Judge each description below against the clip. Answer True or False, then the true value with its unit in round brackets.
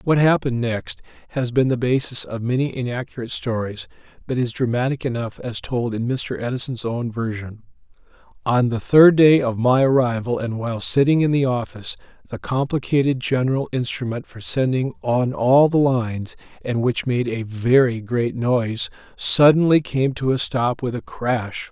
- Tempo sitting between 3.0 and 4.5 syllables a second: False (4.9 syllables/s)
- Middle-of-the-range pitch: False (125 Hz)